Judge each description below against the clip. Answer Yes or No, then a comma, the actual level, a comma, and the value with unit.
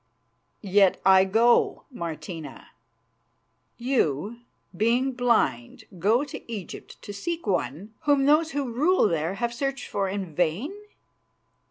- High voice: Yes, high, 215 Hz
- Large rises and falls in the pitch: Yes, wide, 5.9 semitones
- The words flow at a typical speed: No, slow, 120 wpm